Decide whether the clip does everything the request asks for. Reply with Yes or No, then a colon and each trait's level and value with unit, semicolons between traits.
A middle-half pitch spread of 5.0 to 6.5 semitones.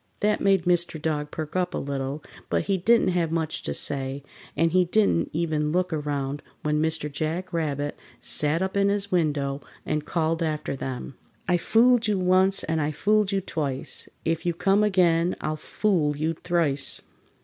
No: average, 3.7 semitones